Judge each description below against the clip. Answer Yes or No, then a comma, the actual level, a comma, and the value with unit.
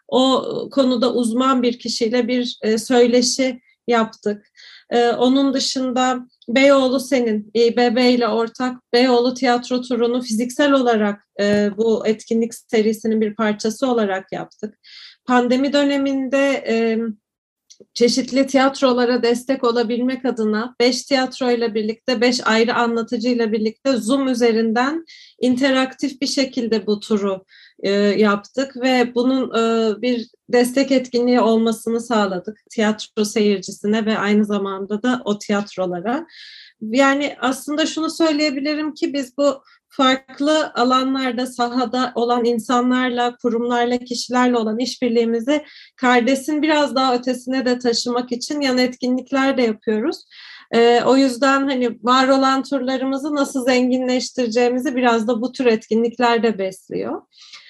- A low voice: No, high, 245 Hz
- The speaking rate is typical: Yes, average, 115 wpm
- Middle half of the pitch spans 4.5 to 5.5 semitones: No, narrow, 2.5 semitones